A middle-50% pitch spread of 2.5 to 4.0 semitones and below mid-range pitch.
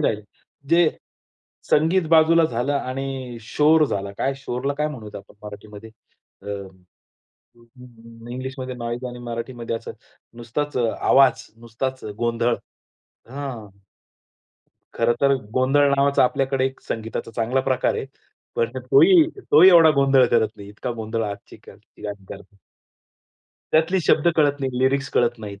Yes: average, 3.7 semitones; low, 130 Hz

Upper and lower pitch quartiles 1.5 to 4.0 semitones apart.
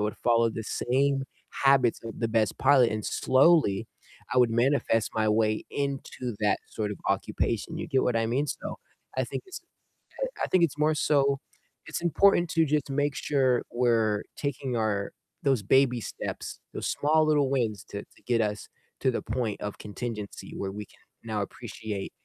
No: average, 4.4 semitones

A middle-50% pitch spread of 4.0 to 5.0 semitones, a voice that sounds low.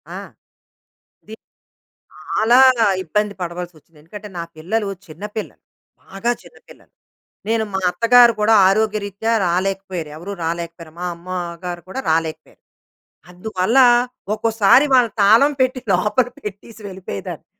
No: average, 4.3 semitones; high, 195 Hz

